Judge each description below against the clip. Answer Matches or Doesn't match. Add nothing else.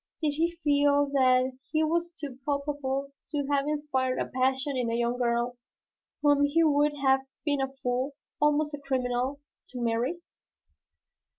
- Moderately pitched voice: Doesn't match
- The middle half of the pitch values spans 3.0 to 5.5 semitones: Doesn't match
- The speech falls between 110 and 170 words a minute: Matches